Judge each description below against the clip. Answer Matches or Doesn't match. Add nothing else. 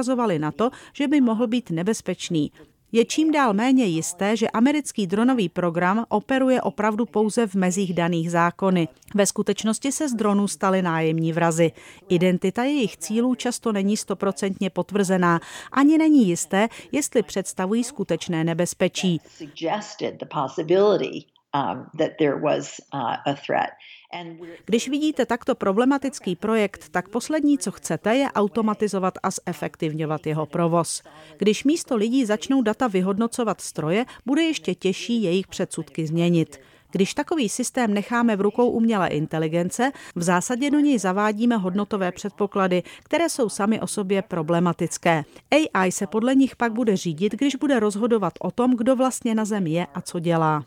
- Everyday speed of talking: Matches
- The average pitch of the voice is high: Matches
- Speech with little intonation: Doesn't match